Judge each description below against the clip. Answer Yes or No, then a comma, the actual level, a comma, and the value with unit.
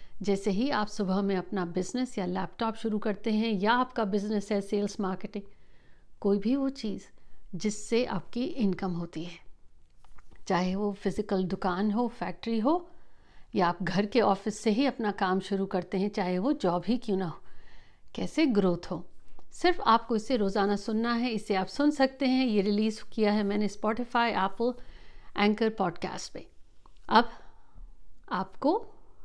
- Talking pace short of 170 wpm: Yes, average, 160 wpm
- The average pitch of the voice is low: No, high, 210 Hz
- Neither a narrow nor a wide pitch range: Yes, average, 3.3 semitones